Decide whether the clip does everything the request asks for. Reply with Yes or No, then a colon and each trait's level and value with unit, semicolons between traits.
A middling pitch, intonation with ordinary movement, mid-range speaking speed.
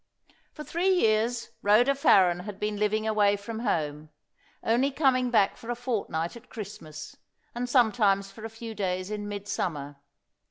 No: high, 215 Hz; average, 3.5 semitones; average, 155 wpm